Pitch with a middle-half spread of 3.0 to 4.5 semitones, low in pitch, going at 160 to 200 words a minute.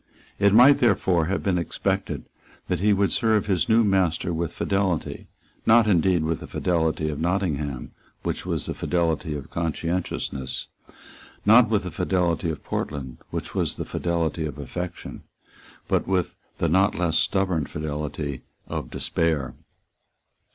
No: average, 3.8 semitones; very low, 85 Hz; average, 145 wpm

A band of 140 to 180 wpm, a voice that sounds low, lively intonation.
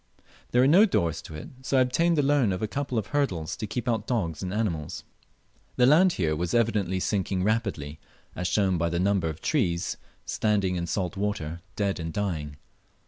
No: average, 200 wpm; low, 100 Hz; wide, 5.9 semitones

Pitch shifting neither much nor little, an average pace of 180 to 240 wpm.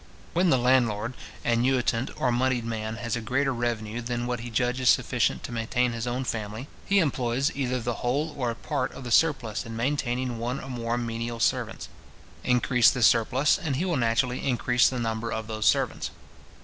No: narrow, 2.0 semitones; average, 190 wpm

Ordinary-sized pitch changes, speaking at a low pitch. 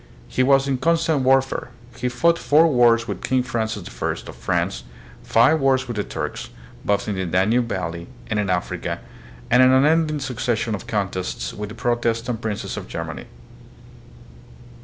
Yes: average, 4.1 semitones; low, 120 Hz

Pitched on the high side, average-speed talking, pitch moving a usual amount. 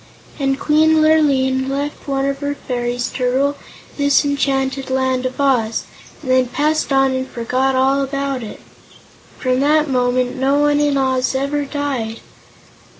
No: very high, 270 Hz; average, 150 wpm; narrow, 1.8 semitones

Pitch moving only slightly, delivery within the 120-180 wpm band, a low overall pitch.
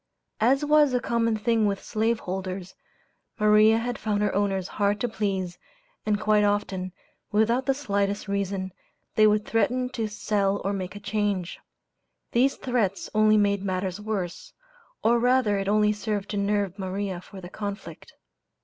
No: narrow, 2.0 semitones; average, 160 wpm; high, 205 Hz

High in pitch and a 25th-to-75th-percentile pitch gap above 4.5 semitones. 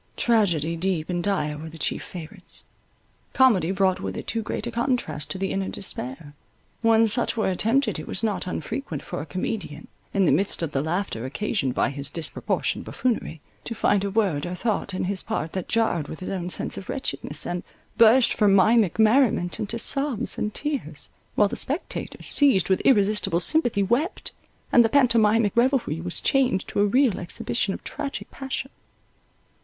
Yes: high, 200 Hz; average, 5.2 semitones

